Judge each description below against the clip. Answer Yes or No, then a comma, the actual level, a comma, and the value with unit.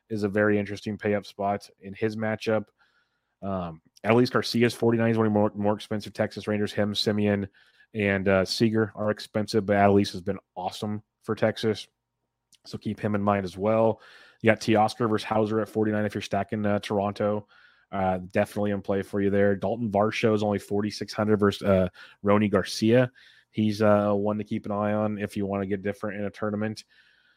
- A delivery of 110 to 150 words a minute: No, average, 195 wpm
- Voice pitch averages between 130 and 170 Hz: No, low, 105 Hz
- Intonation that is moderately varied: No, narrow, 1.4 semitones